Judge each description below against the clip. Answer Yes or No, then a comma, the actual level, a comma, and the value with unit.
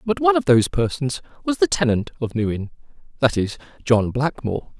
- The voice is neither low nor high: Yes, medium, 145 Hz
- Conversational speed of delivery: Yes, average, 175 wpm